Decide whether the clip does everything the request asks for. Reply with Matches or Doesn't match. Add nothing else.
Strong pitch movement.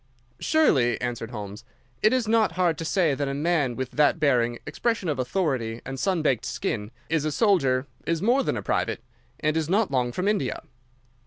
Matches